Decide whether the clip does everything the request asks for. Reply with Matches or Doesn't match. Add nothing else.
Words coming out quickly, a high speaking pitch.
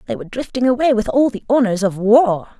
Matches